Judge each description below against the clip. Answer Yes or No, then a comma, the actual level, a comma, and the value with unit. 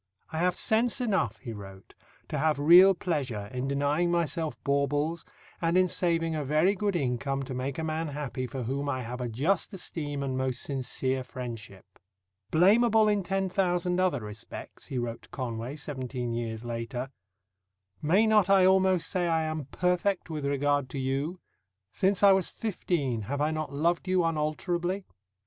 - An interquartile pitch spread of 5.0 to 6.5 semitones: Yes, wide, 5.6 semitones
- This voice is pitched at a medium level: Yes, medium, 150 Hz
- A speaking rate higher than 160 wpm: Yes, average, 170 wpm